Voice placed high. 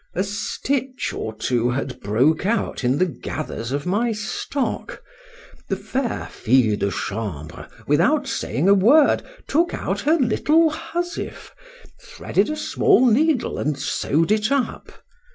Yes: high, 200 Hz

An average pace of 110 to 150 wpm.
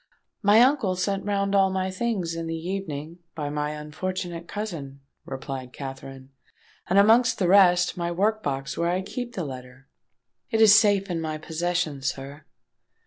No: average, 160 wpm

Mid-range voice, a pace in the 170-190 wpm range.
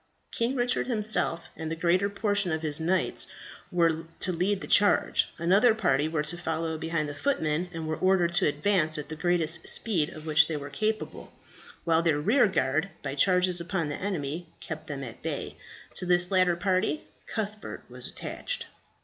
Yes: medium, 170 Hz; average, 175 wpm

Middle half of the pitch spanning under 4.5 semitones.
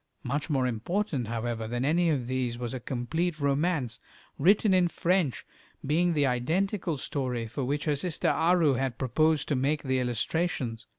No: average, 5.1 semitones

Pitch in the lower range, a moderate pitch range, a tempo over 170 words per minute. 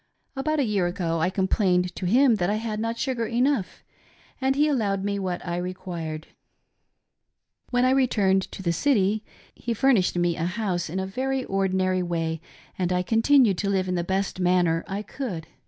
No: high, 195 Hz; average, 4.6 semitones; average, 185 wpm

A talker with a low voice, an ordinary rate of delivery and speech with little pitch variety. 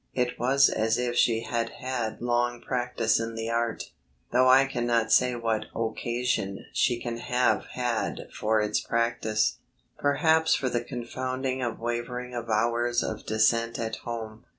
Yes: low, 120 Hz; average, 150 wpm; narrow, 1.6 semitones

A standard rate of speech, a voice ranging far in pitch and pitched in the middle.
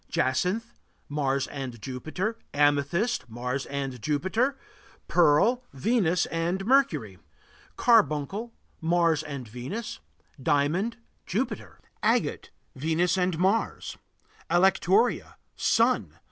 No: slow, 90 wpm; wide, 6.2 semitones; medium, 165 Hz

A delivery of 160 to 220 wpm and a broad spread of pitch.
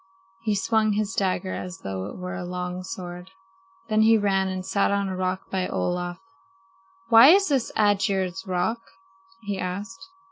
No: average, 165 wpm; average, 2.8 semitones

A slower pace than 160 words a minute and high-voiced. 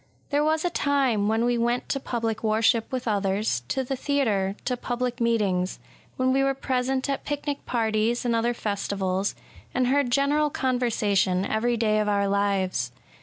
No: average, 175 wpm; high, 235 Hz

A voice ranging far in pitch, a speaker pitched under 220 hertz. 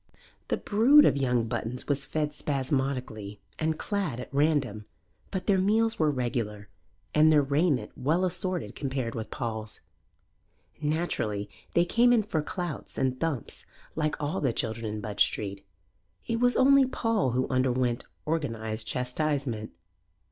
Yes: wide, 6.1 semitones; medium, 140 Hz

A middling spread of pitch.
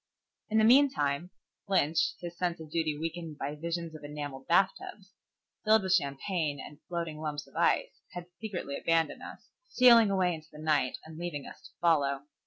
Yes: average, 3.7 semitones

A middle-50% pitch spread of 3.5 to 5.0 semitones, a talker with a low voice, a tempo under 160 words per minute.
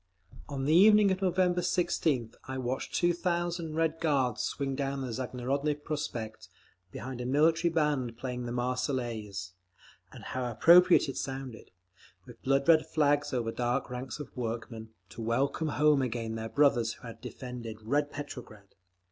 Yes: average, 4.5 semitones; low, 130 Hz; average, 150 wpm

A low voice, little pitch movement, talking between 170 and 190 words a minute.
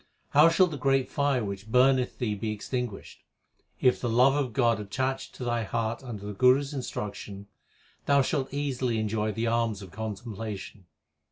No: low, 120 Hz; average, 3.8 semitones; average, 175 wpm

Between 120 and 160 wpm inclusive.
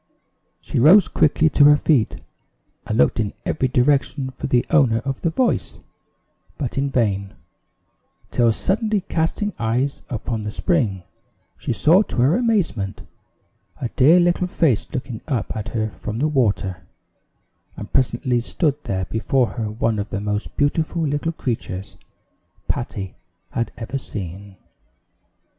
Yes: average, 140 wpm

